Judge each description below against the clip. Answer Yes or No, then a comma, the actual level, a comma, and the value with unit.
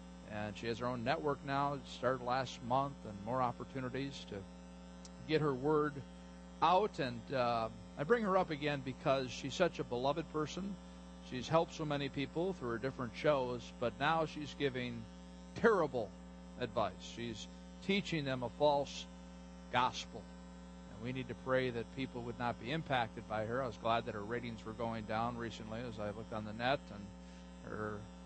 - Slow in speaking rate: No, average, 180 wpm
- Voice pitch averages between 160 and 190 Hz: No, low, 120 Hz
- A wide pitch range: Yes, wide, 7.6 semitones